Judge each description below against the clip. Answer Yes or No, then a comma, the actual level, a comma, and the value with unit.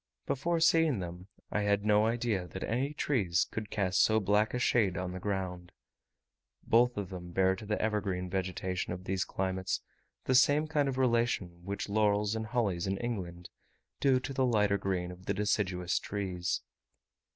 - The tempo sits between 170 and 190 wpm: Yes, average, 175 wpm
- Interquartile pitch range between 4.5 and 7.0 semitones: No, average, 4.0 semitones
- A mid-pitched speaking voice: No, low, 100 Hz